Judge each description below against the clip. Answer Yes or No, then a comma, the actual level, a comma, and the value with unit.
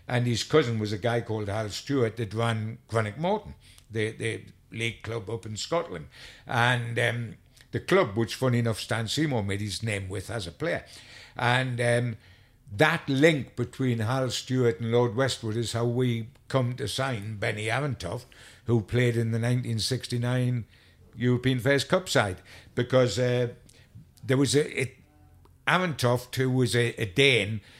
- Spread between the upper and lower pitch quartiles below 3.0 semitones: Yes, narrow, 2.5 semitones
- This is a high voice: No, low, 120 Hz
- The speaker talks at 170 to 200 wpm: No, average, 160 wpm